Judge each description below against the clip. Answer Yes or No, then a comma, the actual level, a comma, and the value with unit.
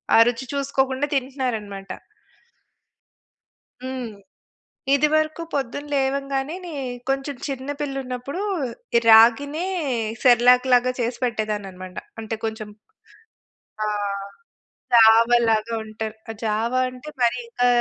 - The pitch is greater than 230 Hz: Yes, high, 245 Hz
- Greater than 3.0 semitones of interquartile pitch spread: Yes, average, 3.6 semitones